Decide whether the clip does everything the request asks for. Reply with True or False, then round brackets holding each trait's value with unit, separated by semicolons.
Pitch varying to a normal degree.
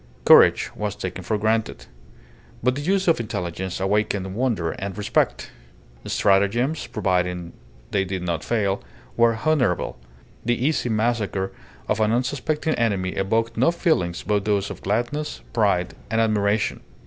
True (3.8 semitones)